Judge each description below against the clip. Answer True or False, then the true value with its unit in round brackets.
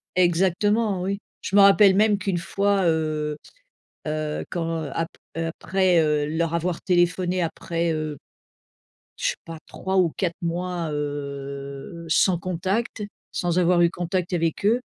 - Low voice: False (175 Hz)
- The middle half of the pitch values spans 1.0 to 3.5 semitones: True (2.8 semitones)